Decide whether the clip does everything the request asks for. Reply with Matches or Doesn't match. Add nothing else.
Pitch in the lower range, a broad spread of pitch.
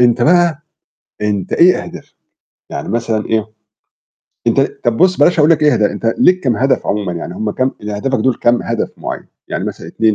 Matches